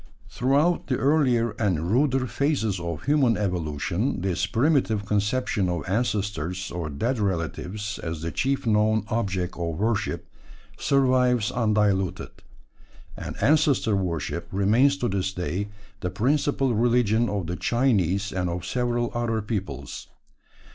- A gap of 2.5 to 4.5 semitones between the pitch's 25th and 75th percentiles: No, average, 5.2 semitones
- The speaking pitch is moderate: No, low, 105 Hz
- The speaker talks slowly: Yes, slow, 125 wpm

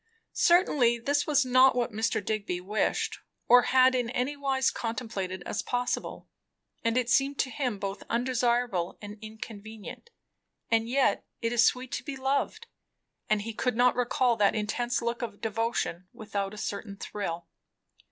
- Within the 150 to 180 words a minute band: Yes, average, 155 wpm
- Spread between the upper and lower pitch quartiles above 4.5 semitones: No, average, 3.3 semitones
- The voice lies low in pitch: No, high, 235 Hz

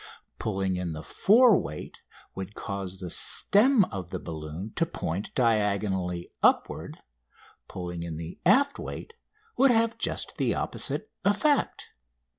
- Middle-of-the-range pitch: No, low, 100 Hz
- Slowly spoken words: Yes, slow, 130 wpm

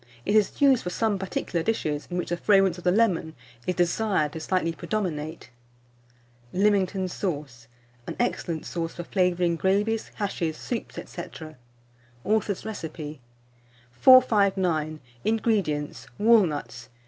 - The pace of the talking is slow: Yes, slow, 125 wpm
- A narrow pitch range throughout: No, average, 4.6 semitones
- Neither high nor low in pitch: Yes, medium, 180 Hz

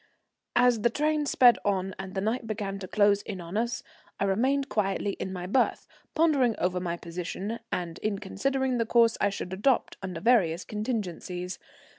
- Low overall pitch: No, high, 205 Hz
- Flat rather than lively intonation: No, average, 4.3 semitones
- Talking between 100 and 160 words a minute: No, average, 175 wpm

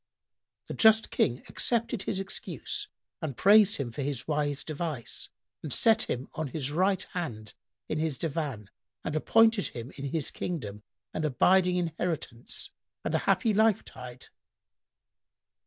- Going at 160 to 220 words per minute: No, average, 140 wpm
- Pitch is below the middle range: No, medium, 155 Hz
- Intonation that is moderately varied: No, wide, 6.2 semitones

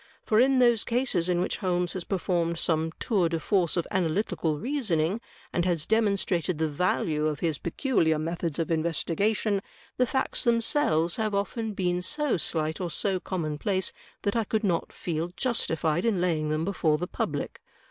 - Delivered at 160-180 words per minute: Yes, average, 170 wpm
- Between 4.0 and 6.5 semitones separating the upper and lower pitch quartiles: Yes, average, 4.6 semitones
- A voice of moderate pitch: Yes, medium, 180 Hz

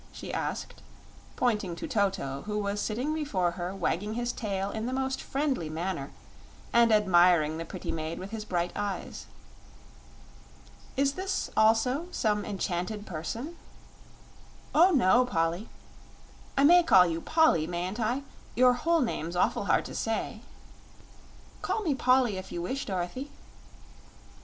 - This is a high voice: Yes, high, 210 Hz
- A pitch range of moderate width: No, wide, 6.6 semitones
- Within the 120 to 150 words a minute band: Yes, average, 140 wpm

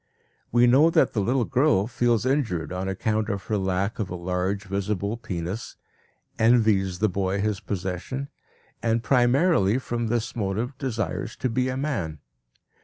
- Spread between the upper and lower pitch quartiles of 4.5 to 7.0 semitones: No, average, 4.1 semitones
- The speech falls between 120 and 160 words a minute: Yes, average, 155 wpm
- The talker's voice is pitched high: No, low, 110 Hz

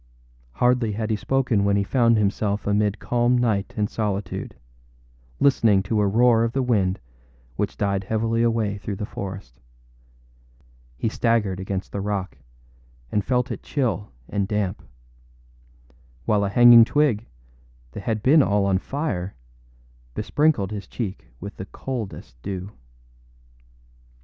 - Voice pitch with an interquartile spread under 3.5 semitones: Yes, average, 3.0 semitones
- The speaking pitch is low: Yes, low, 105 Hz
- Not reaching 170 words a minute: Yes, slow, 135 wpm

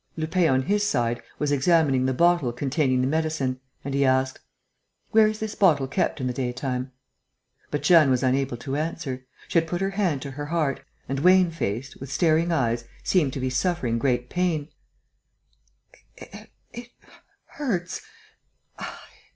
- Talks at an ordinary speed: Yes, average, 155 wpm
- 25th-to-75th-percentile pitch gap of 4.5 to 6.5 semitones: Yes, average, 4.8 semitones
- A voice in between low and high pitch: Yes, medium, 145 Hz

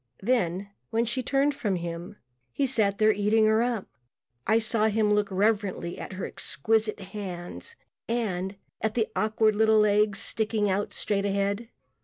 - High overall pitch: Yes, high, 210 Hz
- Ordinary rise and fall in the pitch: No, narrow, 2.0 semitones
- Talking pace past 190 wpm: No, average, 155 wpm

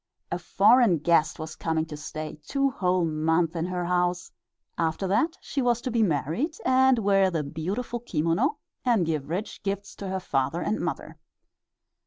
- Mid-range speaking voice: Yes, medium, 180 Hz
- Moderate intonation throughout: No, wide, 5.9 semitones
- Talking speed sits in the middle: Yes, average, 170 wpm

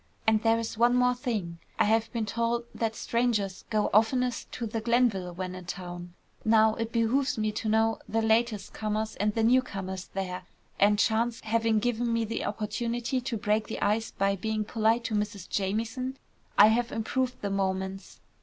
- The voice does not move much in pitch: Yes, narrow, 2.2 semitones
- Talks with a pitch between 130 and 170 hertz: No, high, 220 Hz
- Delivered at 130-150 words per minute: No, average, 175 wpm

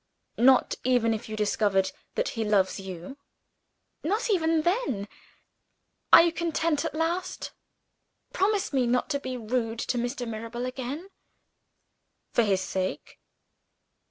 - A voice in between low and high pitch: No, very high, 250 Hz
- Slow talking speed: Yes, slow, 130 wpm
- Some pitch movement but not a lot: No, wide, 6.9 semitones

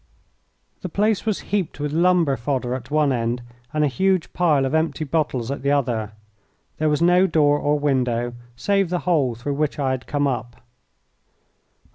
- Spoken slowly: No, average, 175 wpm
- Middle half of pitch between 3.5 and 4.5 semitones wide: Yes, average, 4.2 semitones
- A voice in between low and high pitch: Yes, medium, 145 Hz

